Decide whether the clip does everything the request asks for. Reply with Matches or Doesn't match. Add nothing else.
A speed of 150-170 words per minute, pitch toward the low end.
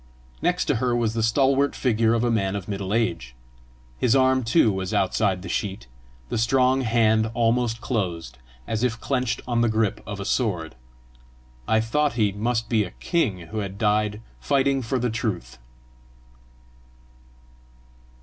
Matches